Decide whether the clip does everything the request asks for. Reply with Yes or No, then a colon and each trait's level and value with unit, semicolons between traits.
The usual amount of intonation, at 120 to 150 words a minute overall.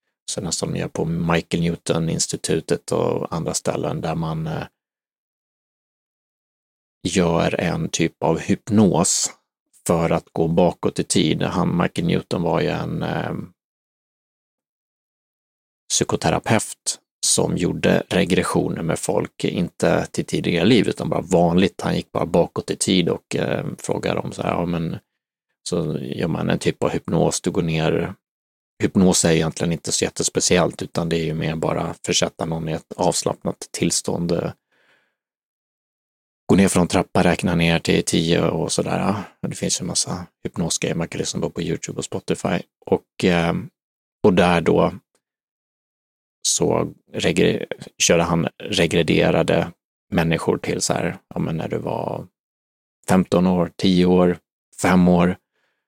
No: narrow, 1.7 semitones; average, 140 wpm